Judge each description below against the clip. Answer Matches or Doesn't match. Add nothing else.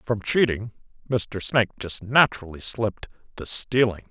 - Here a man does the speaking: Matches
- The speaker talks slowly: Matches